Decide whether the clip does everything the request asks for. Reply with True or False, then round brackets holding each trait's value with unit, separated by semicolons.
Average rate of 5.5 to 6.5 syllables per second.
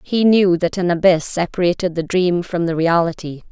False (5.0 syllables/s)